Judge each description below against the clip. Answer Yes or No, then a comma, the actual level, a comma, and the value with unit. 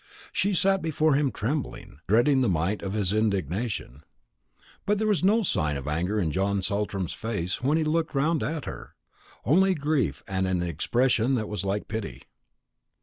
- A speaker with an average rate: Yes, average, 160 wpm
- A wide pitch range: Yes, wide, 8.3 semitones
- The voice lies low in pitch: Yes, low, 110 Hz